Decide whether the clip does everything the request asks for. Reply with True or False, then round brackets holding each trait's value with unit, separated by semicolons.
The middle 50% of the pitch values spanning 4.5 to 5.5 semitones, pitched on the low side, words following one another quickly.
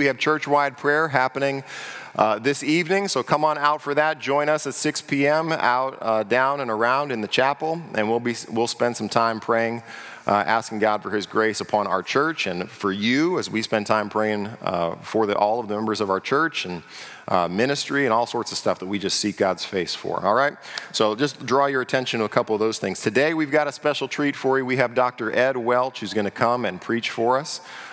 True (4.9 semitones; 125 Hz; 240 wpm)